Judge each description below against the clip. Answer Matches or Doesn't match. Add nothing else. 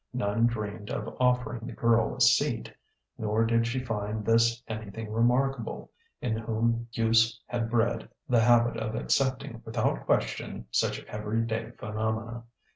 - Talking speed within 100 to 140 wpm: Matches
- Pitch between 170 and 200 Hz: Doesn't match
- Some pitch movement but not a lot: Doesn't match